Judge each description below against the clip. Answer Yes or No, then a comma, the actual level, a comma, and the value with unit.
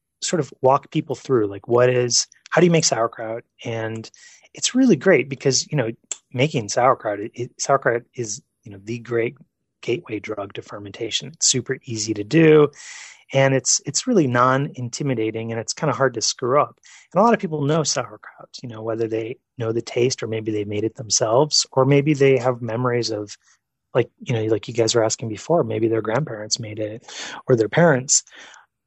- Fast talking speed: No, average, 195 wpm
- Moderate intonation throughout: Yes, average, 3.6 semitones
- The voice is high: No, low, 125 Hz